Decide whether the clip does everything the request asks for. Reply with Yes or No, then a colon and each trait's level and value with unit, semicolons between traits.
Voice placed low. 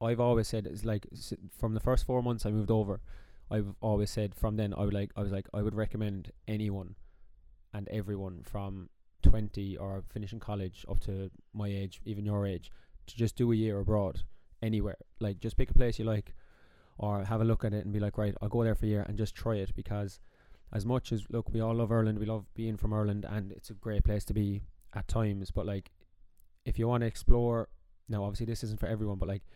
Yes: low, 105 Hz